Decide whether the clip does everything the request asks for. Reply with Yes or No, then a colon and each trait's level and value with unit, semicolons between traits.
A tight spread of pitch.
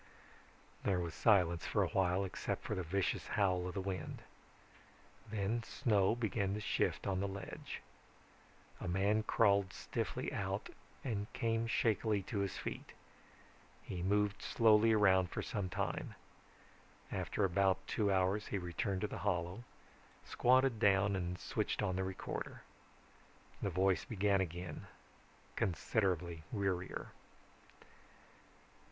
Yes: narrow, 2.3 semitones